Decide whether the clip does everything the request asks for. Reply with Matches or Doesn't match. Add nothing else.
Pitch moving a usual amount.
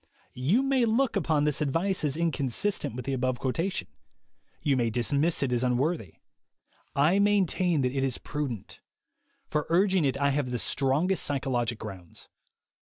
Doesn't match